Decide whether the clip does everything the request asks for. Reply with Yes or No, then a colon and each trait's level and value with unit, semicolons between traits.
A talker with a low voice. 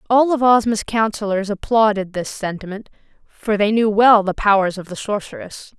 No: high, 210 Hz